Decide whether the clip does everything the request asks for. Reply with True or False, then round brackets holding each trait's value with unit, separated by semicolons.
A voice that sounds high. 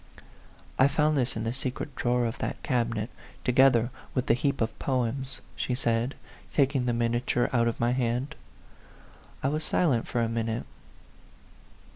False (125 Hz)